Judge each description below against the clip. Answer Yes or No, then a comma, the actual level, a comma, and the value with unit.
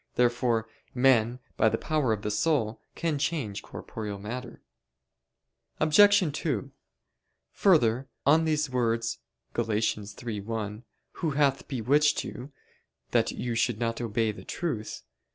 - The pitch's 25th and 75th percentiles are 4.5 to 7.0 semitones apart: Yes, average, 4.8 semitones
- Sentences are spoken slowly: Yes, slow, 120 wpm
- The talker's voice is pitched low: Yes, low, 120 Hz